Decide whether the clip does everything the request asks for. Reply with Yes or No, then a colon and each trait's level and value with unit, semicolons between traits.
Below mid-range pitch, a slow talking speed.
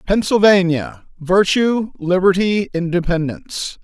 No: medium, 180 Hz; slow, 45 wpm